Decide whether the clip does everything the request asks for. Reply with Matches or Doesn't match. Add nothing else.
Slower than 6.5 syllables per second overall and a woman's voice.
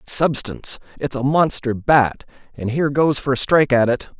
Doesn't match